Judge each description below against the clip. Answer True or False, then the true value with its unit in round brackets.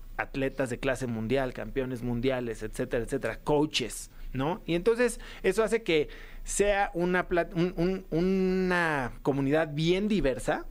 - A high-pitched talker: False (150 Hz)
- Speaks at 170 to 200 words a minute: False (130 wpm)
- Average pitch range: False (5.8 semitones)